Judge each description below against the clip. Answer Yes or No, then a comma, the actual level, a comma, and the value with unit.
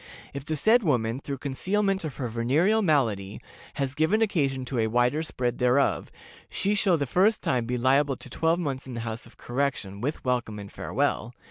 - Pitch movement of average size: Yes, average, 5.0 semitones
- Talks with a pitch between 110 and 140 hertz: Yes, low, 135 Hz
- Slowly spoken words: No, average, 195 wpm